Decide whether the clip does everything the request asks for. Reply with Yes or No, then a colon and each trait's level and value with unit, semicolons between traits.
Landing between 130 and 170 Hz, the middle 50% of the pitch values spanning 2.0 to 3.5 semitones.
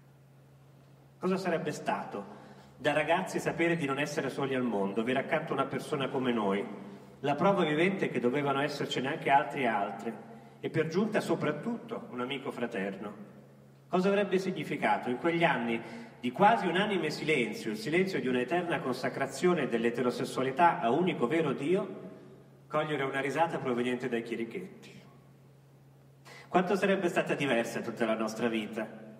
No: medium, 140 Hz; average, 5.3 semitones